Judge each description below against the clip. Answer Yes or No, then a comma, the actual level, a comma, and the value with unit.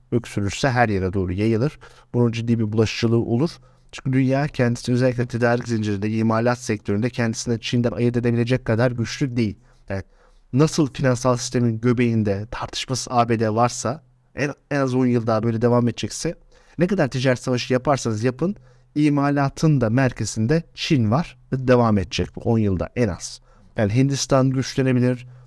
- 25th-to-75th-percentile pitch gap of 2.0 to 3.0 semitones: Yes, narrow, 2.4 semitones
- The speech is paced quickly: Yes, fast, 150 wpm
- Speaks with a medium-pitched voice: No, low, 125 Hz